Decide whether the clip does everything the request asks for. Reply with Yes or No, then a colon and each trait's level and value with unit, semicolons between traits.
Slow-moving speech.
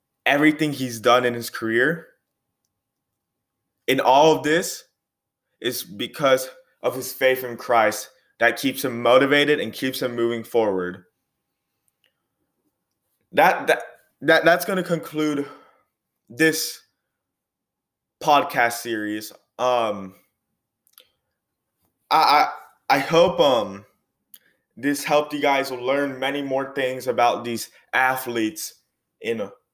Yes: slow, 110 wpm